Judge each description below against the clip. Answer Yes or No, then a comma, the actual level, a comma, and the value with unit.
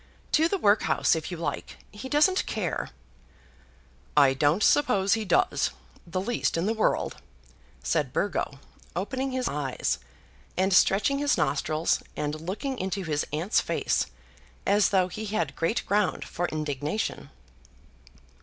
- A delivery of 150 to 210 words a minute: No, slow, 135 wpm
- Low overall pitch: No, high, 190 Hz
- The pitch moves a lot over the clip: Yes, wide, 6.1 semitones